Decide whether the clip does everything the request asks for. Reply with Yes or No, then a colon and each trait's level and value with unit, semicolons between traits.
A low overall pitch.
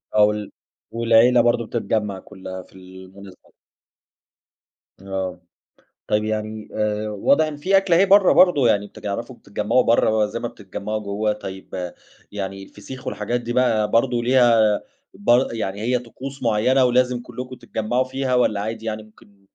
Yes: low, 110 Hz